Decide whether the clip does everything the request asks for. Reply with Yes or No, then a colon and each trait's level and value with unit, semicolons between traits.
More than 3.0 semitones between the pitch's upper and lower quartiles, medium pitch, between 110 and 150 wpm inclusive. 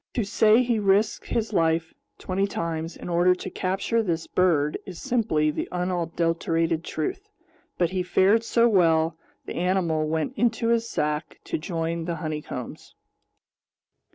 Yes: average, 4.2 semitones; medium, 175 Hz; average, 145 wpm